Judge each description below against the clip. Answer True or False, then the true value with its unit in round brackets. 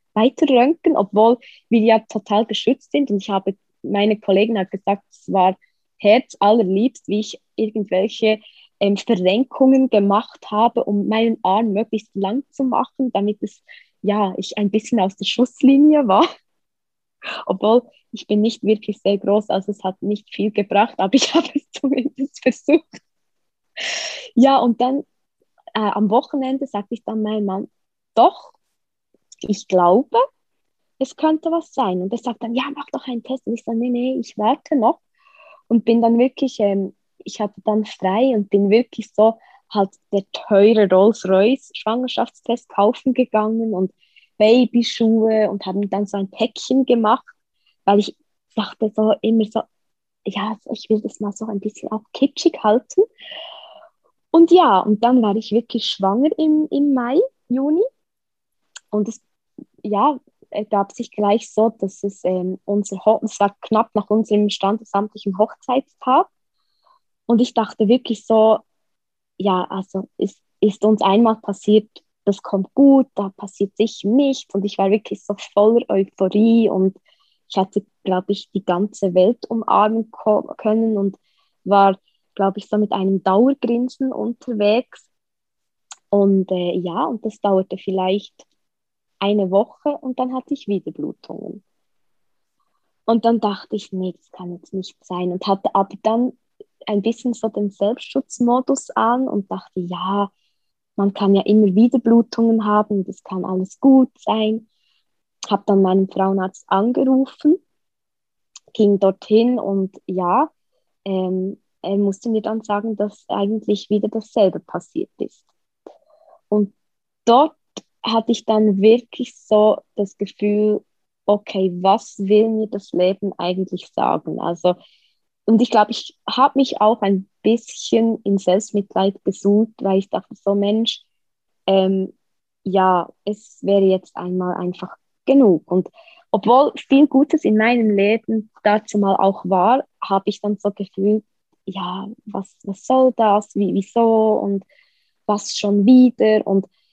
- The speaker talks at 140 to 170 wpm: True (150 wpm)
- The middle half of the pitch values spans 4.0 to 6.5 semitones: False (3.5 semitones)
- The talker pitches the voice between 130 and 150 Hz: False (215 Hz)